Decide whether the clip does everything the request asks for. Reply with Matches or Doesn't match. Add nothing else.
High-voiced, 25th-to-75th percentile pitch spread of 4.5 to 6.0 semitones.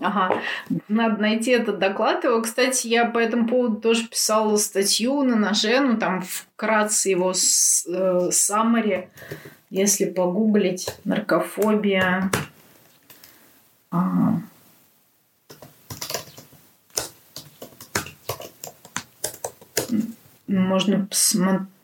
Doesn't match